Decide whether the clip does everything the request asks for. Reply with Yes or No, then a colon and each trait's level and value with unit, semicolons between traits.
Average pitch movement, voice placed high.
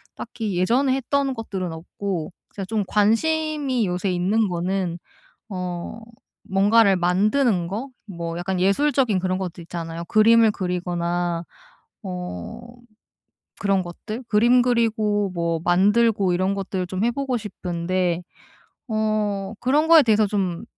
Yes: average, 4.1 semitones; high, 195 Hz